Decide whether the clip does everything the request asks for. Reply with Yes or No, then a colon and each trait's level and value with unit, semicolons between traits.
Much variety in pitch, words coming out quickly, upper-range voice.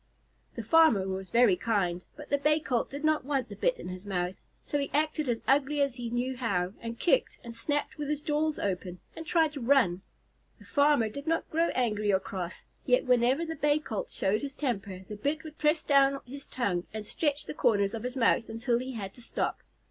Yes: wide, 6.1 semitones; fast, 220 wpm; very high, 250 Hz